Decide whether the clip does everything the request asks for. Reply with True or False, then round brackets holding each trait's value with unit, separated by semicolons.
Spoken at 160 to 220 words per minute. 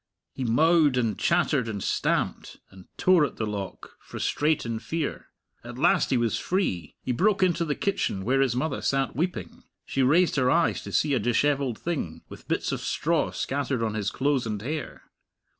True (185 wpm)